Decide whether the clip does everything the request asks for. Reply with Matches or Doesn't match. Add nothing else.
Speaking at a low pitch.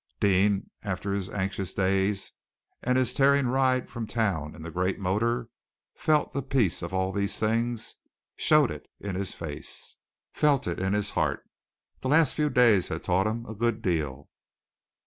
Matches